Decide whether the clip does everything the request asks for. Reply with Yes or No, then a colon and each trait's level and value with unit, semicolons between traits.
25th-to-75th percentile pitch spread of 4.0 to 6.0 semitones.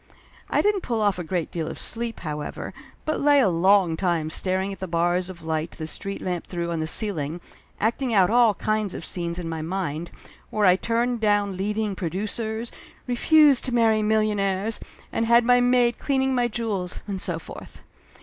Yes: average, 4.8 semitones